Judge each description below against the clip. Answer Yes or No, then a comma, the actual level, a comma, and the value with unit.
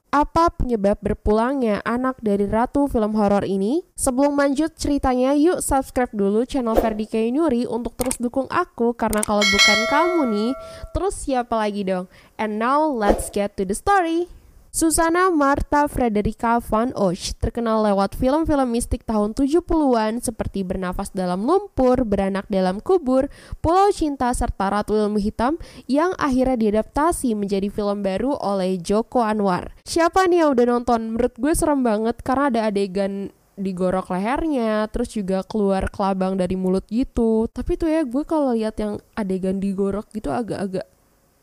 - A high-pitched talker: Yes, high, 230 Hz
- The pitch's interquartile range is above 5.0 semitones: Yes, wide, 5.6 semitones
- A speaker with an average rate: No, fast, 150 wpm